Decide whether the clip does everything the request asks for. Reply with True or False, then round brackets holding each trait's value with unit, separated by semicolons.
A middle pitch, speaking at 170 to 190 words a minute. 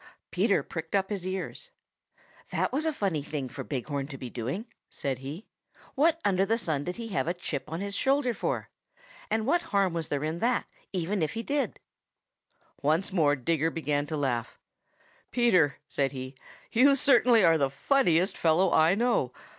True (175 Hz; 180 wpm)